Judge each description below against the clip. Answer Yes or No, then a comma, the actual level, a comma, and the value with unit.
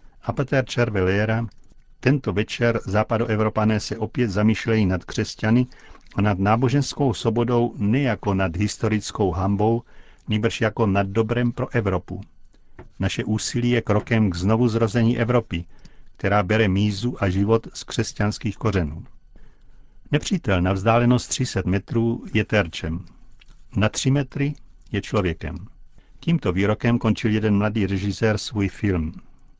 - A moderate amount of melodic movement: Yes, average, 3.2 semitones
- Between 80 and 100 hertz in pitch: No, low, 110 Hz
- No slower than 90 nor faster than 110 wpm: No, average, 120 wpm